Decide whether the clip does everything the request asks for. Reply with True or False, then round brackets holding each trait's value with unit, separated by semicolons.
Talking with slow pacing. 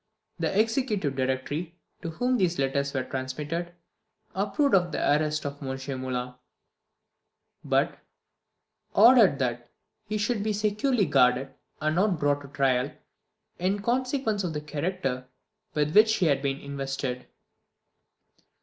True (130 wpm)